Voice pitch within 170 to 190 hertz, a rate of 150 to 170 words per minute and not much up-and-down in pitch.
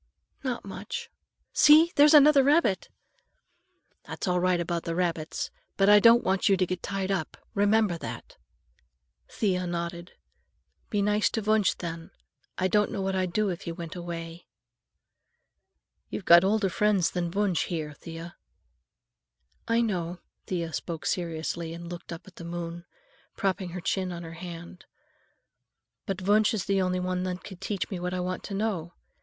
No: medium, 185 Hz; average, 165 wpm; average, 3.2 semitones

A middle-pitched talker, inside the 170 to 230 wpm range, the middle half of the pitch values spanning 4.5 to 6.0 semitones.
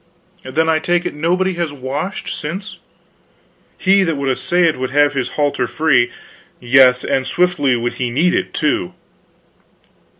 No: medium, 150 Hz; average, 155 wpm; average, 5.0 semitones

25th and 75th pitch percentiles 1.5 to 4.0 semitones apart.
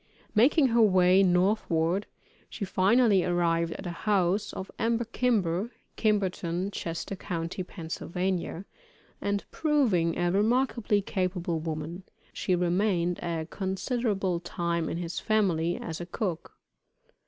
Yes: average, 3.6 semitones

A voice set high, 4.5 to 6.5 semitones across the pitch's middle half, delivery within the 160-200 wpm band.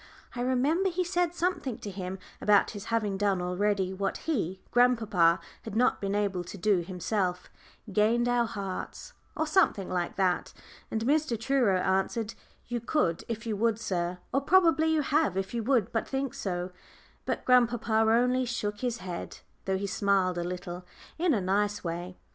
Yes: high, 210 Hz; average, 4.8 semitones; average, 170 wpm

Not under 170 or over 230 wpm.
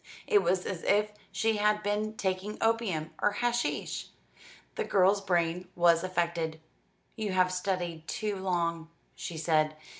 No: average, 140 wpm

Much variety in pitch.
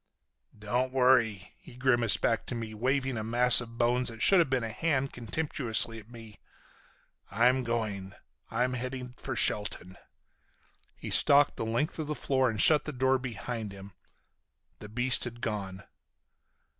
No: average, 2.8 semitones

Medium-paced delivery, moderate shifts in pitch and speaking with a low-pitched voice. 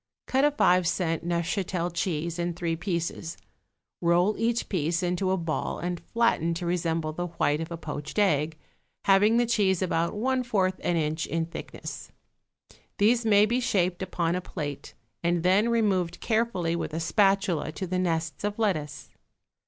No: average, 165 wpm; average, 3.5 semitones; medium, 175 Hz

